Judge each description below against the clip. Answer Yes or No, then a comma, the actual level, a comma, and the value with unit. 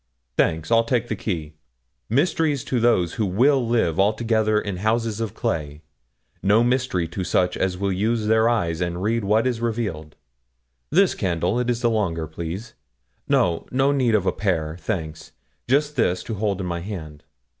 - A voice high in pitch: No, low, 105 Hz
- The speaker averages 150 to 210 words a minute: Yes, average, 175 wpm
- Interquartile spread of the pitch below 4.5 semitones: No, average, 5.1 semitones